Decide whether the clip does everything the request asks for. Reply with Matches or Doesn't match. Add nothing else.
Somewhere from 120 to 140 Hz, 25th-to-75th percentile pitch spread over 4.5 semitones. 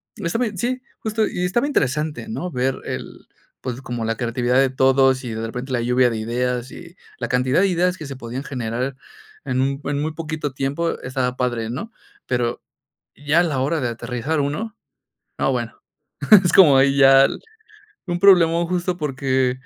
Matches